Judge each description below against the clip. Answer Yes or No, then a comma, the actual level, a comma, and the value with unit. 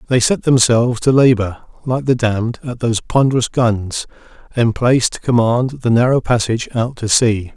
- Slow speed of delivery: No, average, 165 wpm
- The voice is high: No, low, 120 Hz